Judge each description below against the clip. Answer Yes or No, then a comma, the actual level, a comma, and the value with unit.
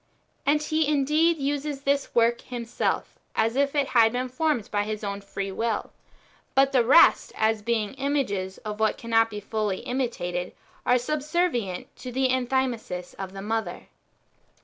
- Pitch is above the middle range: Yes, high, 240 Hz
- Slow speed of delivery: No, average, 155 wpm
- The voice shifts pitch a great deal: No, average, 4.6 semitones